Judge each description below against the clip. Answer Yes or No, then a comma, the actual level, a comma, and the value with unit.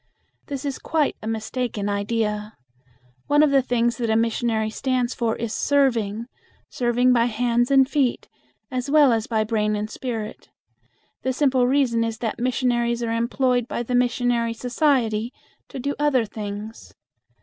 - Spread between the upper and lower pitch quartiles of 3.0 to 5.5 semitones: No, narrow, 2.4 semitones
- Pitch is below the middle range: No, high, 240 Hz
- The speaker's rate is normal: Yes, average, 155 wpm